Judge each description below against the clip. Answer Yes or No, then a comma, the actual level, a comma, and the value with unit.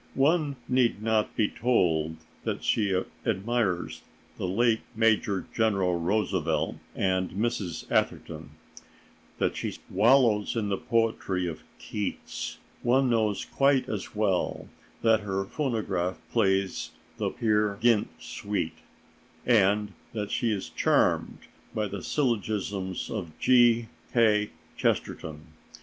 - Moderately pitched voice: No, low, 105 Hz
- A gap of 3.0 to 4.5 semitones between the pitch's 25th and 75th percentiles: Yes, average, 3.7 semitones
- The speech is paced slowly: Yes, slow, 115 wpm